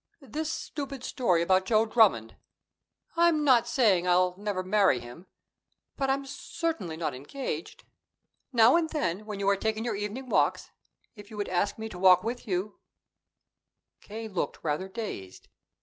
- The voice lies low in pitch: No, high, 210 Hz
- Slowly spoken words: No, average, 160 wpm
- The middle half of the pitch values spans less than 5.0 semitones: No, wide, 5.5 semitones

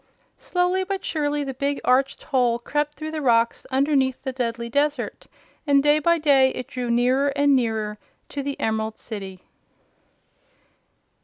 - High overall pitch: Yes, very high, 270 Hz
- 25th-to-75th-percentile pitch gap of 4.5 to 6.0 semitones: No, average, 3.7 semitones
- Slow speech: No, average, 150 wpm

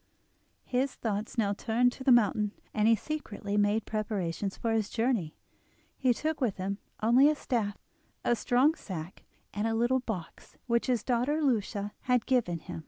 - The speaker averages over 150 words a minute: Yes, average, 170 wpm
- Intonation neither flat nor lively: Yes, average, 3.5 semitones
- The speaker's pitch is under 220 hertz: No, high, 225 Hz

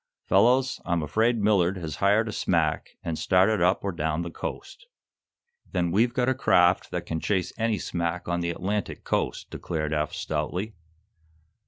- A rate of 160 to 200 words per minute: Yes, average, 165 wpm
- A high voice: No, very low, 90 Hz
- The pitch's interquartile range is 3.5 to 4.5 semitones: Yes, average, 4.2 semitones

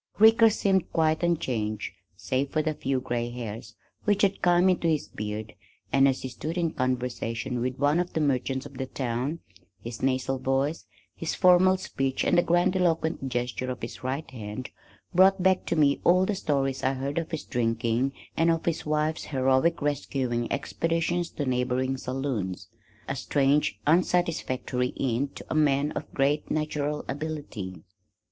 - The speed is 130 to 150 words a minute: No, average, 165 wpm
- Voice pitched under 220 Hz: Yes, medium, 140 Hz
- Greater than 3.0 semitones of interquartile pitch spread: Yes, average, 4.4 semitones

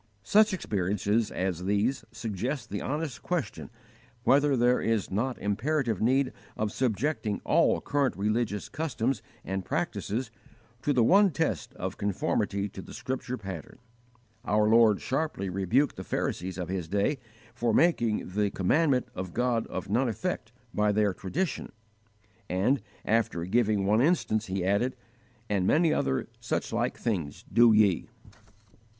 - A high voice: No, low, 110 Hz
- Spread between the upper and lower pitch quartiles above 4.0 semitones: Yes, average, 4.9 semitones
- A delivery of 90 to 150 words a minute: Yes, average, 140 wpm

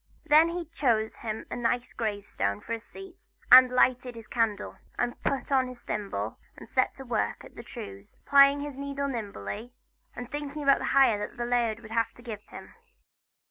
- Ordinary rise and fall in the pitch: Yes, average, 4.2 semitones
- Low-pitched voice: No, high, 245 Hz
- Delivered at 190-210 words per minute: Yes, average, 200 wpm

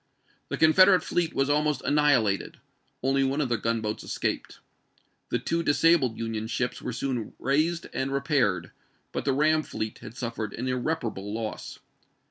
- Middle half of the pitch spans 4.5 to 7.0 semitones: Yes, average, 4.8 semitones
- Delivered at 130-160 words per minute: Yes, average, 150 wpm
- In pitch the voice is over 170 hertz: No, low, 130 Hz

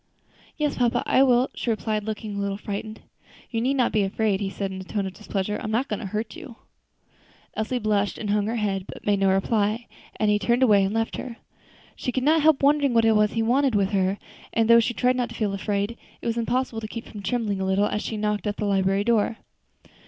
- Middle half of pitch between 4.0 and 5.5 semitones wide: No, average, 2.8 semitones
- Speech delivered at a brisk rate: Yes, fast, 240 wpm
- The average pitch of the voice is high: Yes, high, 215 Hz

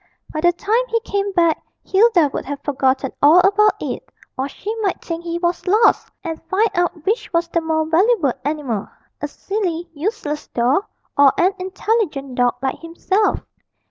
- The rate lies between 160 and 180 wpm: Yes, average, 170 wpm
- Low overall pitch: No, very high, 340 Hz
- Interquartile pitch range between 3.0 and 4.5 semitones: No, average, 5.3 semitones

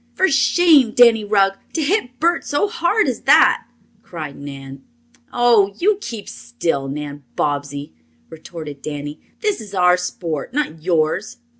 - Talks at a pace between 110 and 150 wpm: Yes, average, 140 wpm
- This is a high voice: Yes, high, 195 Hz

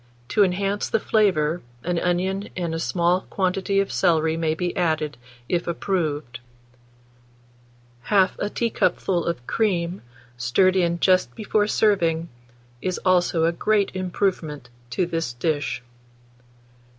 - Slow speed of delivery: Yes, slow, 125 wpm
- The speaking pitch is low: No, medium, 175 Hz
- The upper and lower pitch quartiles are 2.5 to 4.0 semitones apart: Yes, average, 2.9 semitones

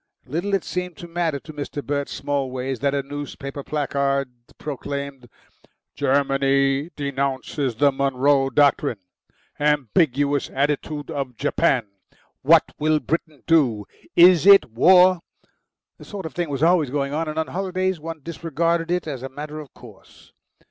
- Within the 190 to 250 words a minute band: No, average, 140 wpm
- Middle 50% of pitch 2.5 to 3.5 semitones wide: Yes, average, 3.1 semitones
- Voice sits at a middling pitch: Yes, medium, 145 Hz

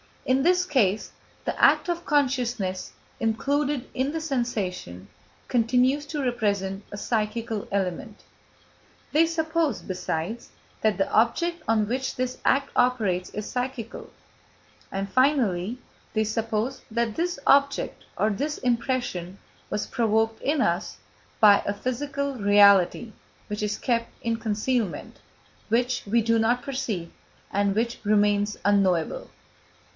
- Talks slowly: Yes, slow, 125 wpm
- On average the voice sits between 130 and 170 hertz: No, high, 230 Hz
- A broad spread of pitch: No, average, 4.3 semitones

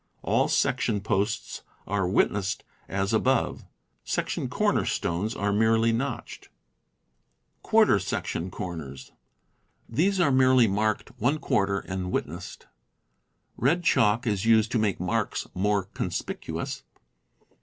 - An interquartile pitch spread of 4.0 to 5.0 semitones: No, average, 3.4 semitones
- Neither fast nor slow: No, slow, 110 wpm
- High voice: No, low, 105 Hz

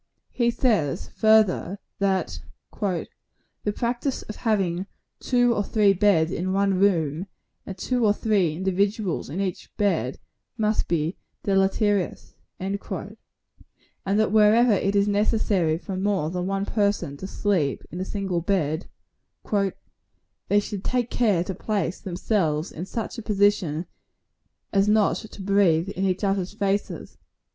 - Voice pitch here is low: No, high, 195 Hz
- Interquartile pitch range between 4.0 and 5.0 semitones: No, narrow, 2.6 semitones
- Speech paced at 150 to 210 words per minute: No, slow, 135 wpm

